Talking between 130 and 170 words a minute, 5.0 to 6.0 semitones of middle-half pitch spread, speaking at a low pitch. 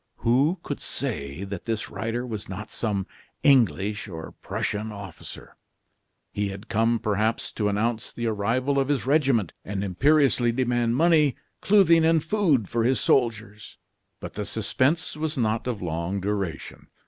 No: average, 150 wpm; average, 4.6 semitones; low, 115 Hz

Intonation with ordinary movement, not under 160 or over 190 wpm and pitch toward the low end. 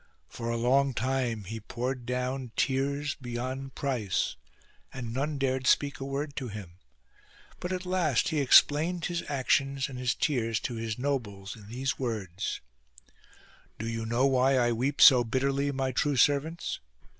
Yes: average, 3.0 semitones; average, 165 wpm; low, 130 Hz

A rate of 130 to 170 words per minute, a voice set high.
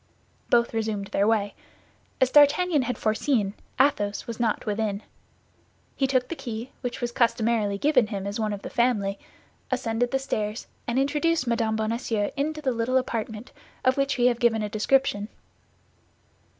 Yes: average, 160 wpm; high, 235 Hz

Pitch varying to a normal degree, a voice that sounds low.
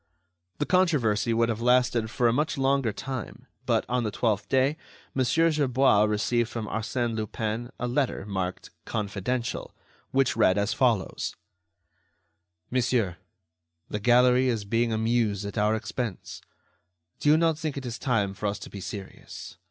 Yes: average, 3.5 semitones; low, 115 Hz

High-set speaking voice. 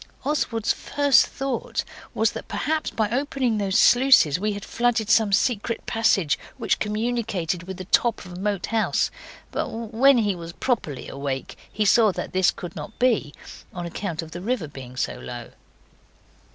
Yes: high, 210 Hz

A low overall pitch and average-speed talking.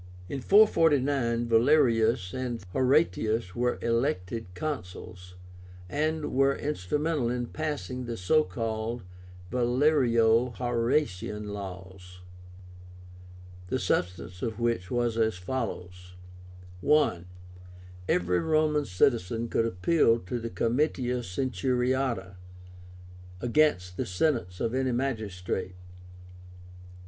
No: low, 120 Hz; slow, 95 wpm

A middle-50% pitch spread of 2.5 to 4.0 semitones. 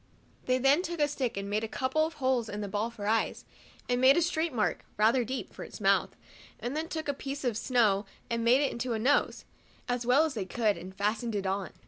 No: average, 4.4 semitones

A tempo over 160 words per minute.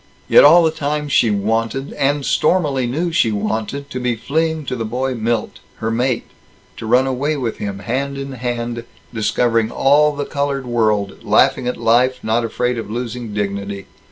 Yes: average, 175 wpm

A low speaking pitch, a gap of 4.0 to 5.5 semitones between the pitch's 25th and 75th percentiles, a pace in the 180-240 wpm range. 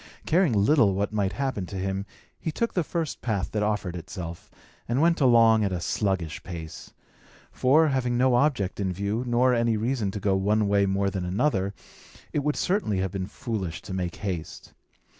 Yes: low, 105 Hz; average, 4.8 semitones; average, 185 wpm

